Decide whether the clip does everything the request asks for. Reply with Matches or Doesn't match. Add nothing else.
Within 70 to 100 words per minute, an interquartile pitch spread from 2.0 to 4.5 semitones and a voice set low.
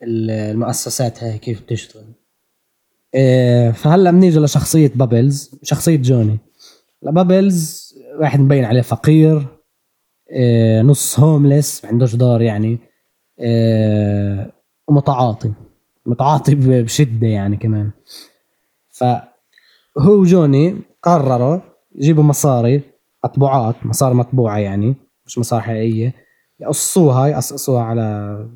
Matches